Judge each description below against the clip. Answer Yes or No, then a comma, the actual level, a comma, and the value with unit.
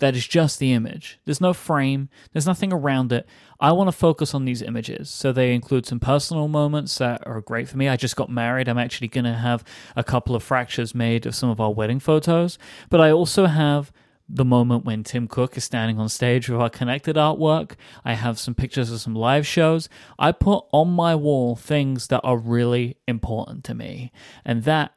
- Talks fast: Yes, fast, 215 wpm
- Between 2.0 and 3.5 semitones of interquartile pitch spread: No, average, 3.9 semitones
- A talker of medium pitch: No, low, 130 Hz